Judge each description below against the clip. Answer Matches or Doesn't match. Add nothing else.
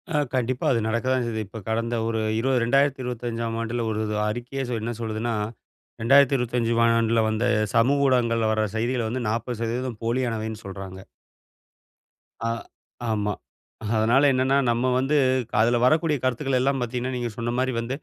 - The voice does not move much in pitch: Matches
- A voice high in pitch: Doesn't match